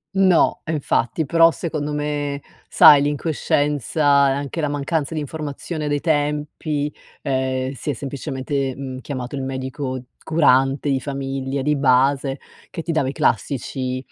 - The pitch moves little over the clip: Yes, narrow, 1.9 semitones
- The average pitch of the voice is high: No, medium, 140 Hz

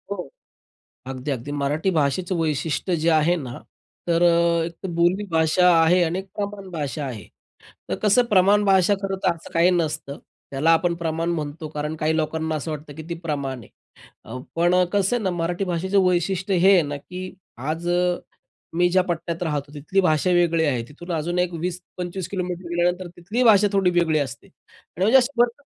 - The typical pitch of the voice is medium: Yes, medium, 170 Hz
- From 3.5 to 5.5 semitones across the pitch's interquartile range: No, average, 2.9 semitones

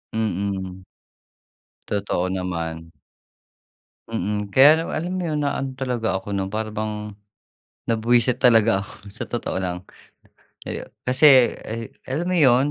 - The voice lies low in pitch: Yes, low, 110 Hz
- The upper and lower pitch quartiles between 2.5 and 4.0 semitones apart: No, average, 4.6 semitones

